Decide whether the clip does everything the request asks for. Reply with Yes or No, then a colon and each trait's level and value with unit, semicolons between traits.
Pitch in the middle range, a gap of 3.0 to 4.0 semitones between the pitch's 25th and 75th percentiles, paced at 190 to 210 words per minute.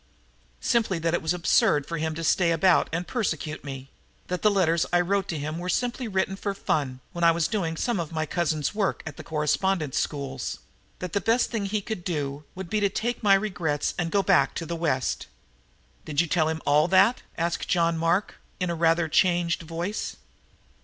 Yes: medium, 170 Hz; average, 3.4 semitones; average, 200 wpm